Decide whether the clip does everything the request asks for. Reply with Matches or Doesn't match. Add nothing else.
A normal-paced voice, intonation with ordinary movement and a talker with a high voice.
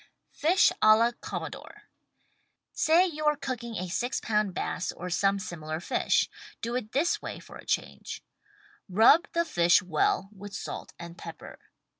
Doesn't match